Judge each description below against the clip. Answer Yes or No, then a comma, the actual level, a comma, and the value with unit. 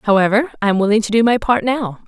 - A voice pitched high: Yes, high, 220 Hz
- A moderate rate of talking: No, fast, 260 wpm